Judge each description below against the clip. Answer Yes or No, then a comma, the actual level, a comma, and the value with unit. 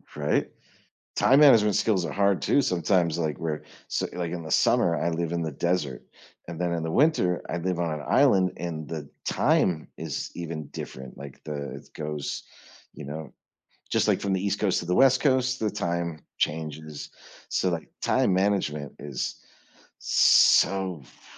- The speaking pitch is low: Yes, very low, 85 Hz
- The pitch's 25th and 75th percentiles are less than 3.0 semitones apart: No, average, 3.5 semitones